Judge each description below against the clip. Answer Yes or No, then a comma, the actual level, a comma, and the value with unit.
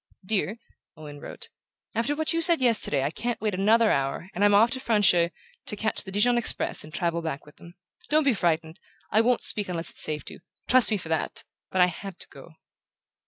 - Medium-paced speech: No, fast, 210 wpm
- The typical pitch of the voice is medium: No, high, 200 Hz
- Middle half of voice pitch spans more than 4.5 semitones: Yes, wide, 5.6 semitones